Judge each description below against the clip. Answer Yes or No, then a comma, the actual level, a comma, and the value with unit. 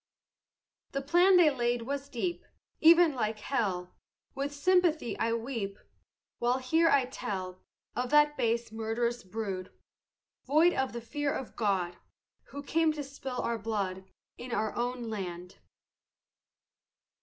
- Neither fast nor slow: No, slow, 130 wpm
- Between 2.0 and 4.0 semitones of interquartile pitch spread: No, average, 4.6 semitones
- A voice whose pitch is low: No, high, 245 Hz